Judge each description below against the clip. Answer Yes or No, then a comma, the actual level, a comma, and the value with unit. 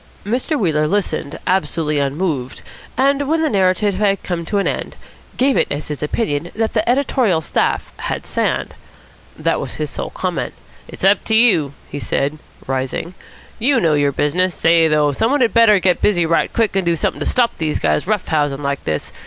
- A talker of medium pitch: Yes, medium, 180 Hz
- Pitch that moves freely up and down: Yes, wide, 6.6 semitones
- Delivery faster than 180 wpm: Yes, average, 195 wpm